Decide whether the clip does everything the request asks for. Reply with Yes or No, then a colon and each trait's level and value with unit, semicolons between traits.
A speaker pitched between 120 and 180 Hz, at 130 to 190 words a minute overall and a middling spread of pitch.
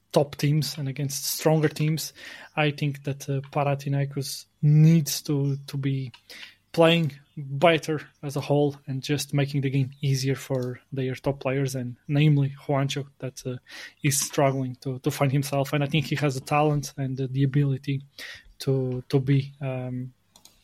No: medium, 140 Hz; average, 165 wpm; narrow, 1.6 semitones